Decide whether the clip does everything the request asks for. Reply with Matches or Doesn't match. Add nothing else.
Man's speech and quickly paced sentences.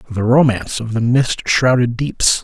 Doesn't match